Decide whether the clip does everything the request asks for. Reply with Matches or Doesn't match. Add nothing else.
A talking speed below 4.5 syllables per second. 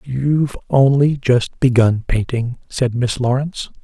Matches